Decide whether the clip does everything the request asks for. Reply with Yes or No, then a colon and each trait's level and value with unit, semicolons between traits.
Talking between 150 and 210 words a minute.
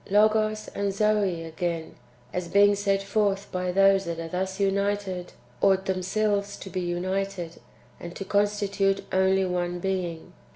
No: average, 140 wpm